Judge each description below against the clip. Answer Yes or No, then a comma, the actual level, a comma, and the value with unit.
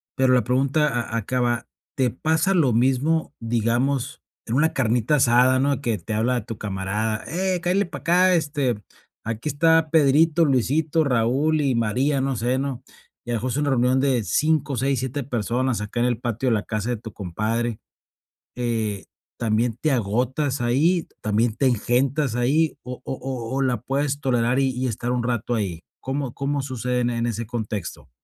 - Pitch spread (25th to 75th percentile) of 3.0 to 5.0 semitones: Yes, average, 3.3 semitones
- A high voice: No, low, 125 Hz